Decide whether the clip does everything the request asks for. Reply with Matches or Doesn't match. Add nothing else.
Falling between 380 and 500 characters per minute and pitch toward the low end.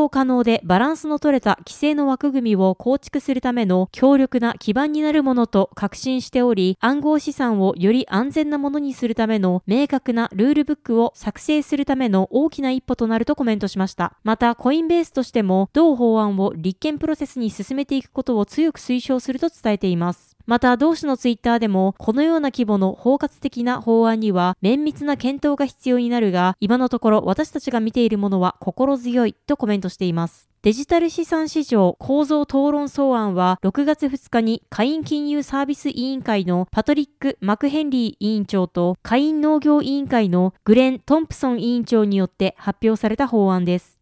Doesn't match